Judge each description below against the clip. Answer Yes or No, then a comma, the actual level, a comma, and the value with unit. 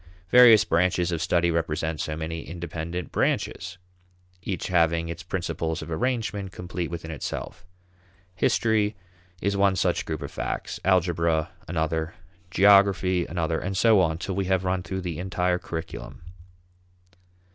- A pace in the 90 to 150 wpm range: Yes, slow, 135 wpm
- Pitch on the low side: Yes, very low, 90 Hz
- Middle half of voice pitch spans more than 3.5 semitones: No, narrow, 2.4 semitones